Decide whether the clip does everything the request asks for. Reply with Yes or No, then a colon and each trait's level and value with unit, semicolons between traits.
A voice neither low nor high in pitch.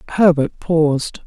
Yes: medium, 160 Hz